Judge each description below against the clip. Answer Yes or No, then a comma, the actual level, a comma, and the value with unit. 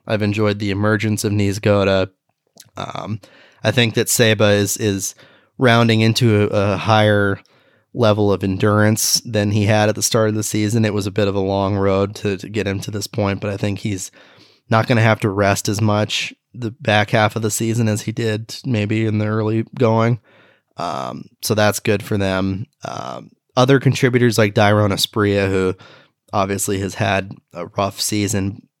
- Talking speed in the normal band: Yes, average, 190 wpm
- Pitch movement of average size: No, narrow, 1.8 semitones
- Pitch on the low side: Yes, low, 105 Hz